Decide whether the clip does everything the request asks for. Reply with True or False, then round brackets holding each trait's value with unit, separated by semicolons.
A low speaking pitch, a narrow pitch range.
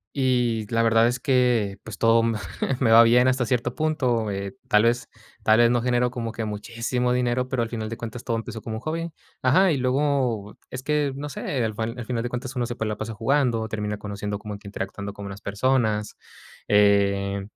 False (115 Hz; 3.0 semitones)